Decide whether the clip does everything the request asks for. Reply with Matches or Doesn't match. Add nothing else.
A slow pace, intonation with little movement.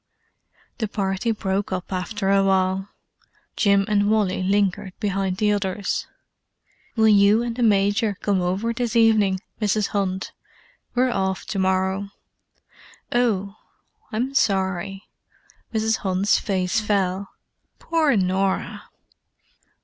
Matches